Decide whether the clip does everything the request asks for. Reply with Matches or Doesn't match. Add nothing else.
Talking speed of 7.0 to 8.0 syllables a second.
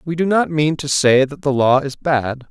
Doesn't match